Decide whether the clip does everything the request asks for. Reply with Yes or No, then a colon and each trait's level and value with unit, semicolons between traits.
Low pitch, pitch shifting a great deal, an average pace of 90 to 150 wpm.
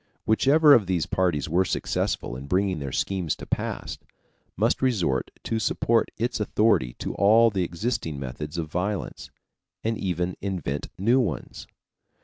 Yes: very low, 95 Hz; wide, 5.8 semitones; average, 145 wpm